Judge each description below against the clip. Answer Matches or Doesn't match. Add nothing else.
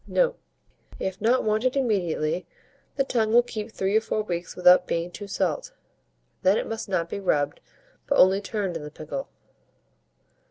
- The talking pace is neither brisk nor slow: Matches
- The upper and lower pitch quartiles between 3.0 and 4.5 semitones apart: Matches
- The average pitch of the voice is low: Doesn't match